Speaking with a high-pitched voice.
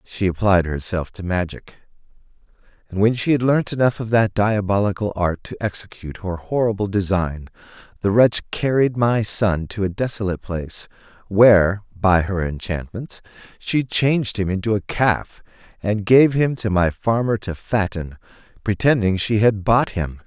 No: low, 100 Hz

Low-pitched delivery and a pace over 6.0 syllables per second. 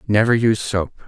Yes: low, 110 Hz; 6.2 syllables/s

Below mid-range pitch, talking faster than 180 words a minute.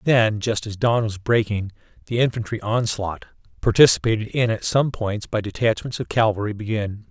No: low, 110 Hz; average, 160 wpm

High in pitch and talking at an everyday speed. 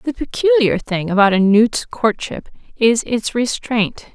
Yes: high, 225 Hz; average, 145 wpm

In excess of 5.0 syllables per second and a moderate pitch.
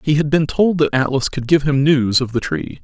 Yes: 5.2 syllables/s; medium, 145 Hz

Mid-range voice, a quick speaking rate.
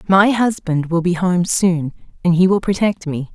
No: medium, 180 Hz; average, 195 wpm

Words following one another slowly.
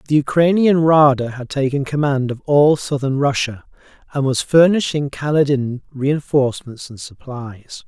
Yes: slow, 130 wpm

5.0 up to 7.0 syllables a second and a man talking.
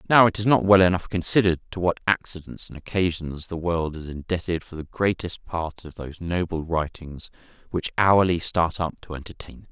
Yes: 5.4 syllables/s; male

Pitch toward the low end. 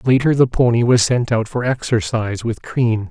Yes: low, 120 Hz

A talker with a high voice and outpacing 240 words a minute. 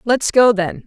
No: high, 215 Hz; fast, 210 wpm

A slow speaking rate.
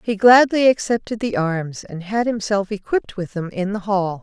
No: average, 200 wpm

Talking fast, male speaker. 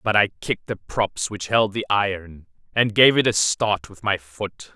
Yes: fast, 215 wpm; male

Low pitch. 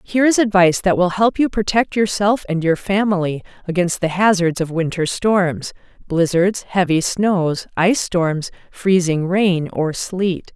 No: medium, 185 Hz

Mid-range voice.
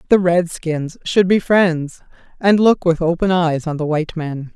Yes: medium, 170 Hz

